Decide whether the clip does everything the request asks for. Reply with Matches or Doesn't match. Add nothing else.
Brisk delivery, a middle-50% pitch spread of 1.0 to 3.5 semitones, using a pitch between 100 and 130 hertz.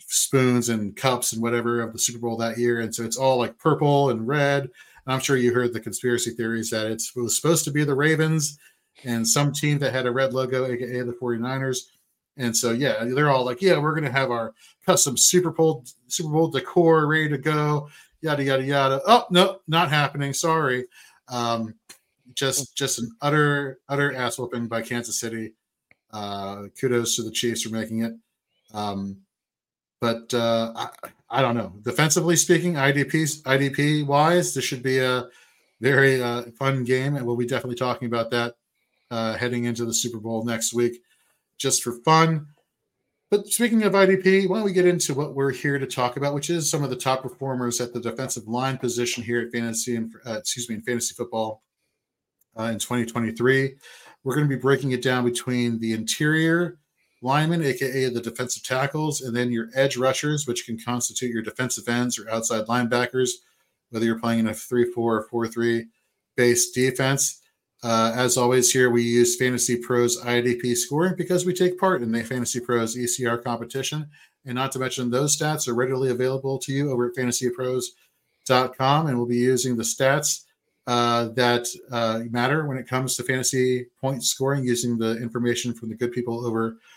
Doesn't match